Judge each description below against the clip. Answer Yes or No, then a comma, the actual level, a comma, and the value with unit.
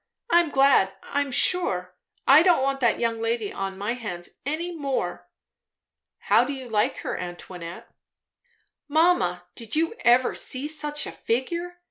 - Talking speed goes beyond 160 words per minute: No, average, 145 wpm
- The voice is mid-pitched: No, very high, 260 Hz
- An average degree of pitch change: No, wide, 6.6 semitones